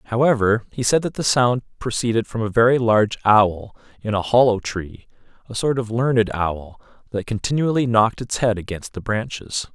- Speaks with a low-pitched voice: Yes, low, 115 Hz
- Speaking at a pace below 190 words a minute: Yes, average, 180 wpm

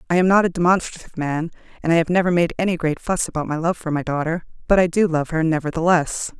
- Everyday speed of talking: No, fast, 245 wpm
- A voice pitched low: No, medium, 170 Hz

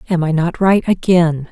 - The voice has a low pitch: No, medium, 170 Hz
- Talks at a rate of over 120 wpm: Yes, average, 200 wpm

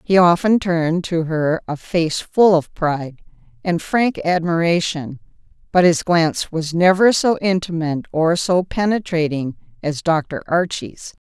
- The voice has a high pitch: No, medium, 170 Hz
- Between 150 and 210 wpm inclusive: No, average, 140 wpm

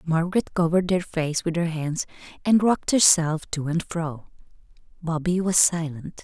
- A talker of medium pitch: Yes, medium, 165 Hz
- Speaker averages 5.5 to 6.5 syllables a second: No, 4.9 syllables/s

